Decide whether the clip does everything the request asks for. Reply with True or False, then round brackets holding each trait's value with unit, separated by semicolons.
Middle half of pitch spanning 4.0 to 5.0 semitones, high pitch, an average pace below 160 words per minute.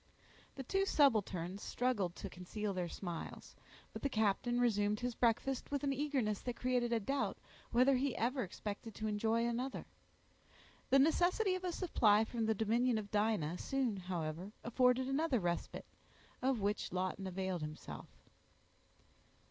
True (4.6 semitones; 225 Hz; 150 wpm)